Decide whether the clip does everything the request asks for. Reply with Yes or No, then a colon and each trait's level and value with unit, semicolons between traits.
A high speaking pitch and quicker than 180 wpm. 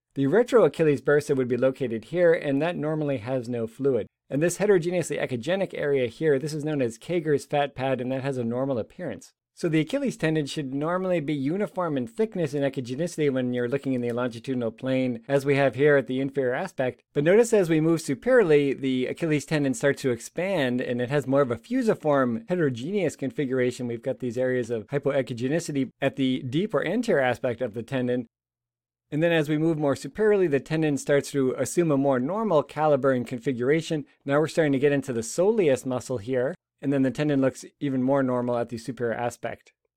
No: medium, 140 Hz; fast, 205 wpm